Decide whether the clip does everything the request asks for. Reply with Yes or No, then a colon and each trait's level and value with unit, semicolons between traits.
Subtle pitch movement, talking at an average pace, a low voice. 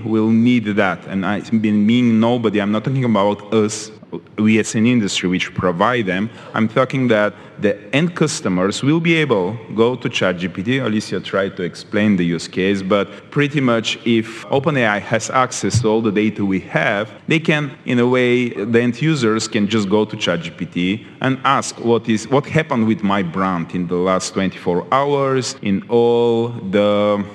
No: average, 3.3 semitones; average, 185 wpm; low, 110 Hz